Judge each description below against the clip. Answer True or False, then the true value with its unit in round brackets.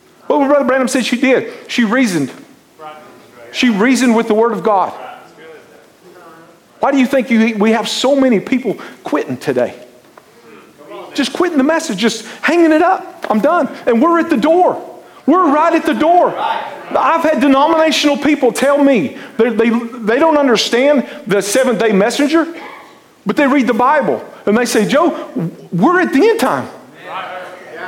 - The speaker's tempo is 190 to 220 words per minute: False (165 wpm)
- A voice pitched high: True (270 Hz)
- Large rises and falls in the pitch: False (5.0 semitones)